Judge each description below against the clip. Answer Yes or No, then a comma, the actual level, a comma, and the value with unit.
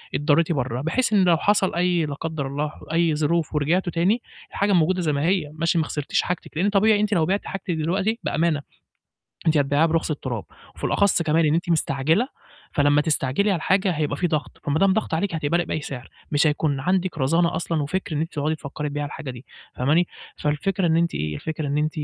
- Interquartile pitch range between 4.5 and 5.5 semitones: No, average, 3.4 semitones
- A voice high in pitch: No, medium, 160 Hz